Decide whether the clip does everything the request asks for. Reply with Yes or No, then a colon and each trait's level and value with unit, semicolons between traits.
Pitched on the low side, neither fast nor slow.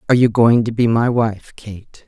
No: low, 115 Hz; fast, 230 wpm